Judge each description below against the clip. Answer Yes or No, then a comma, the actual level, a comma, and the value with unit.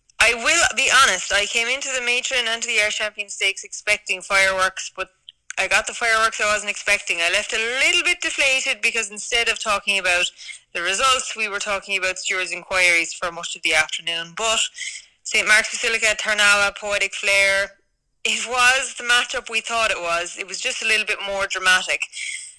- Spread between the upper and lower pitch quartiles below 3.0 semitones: No, average, 3.3 semitones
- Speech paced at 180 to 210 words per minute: Yes, average, 190 wpm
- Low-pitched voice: No, high, 210 Hz